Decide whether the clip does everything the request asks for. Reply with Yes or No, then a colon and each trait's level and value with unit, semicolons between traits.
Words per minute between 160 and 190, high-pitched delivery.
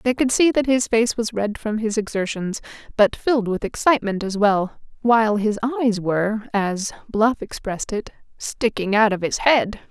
Yes: average, 180 wpm; high, 215 Hz